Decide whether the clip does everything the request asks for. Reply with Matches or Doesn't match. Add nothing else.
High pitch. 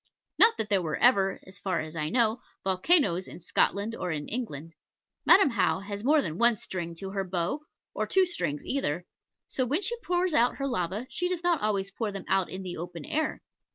Matches